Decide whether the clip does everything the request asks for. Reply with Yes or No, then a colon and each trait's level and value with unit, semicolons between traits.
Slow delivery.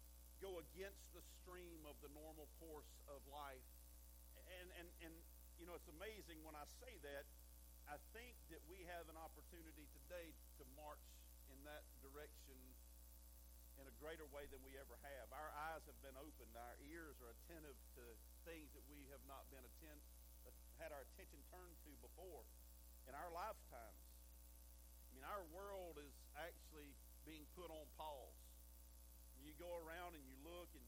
No: average, 160 wpm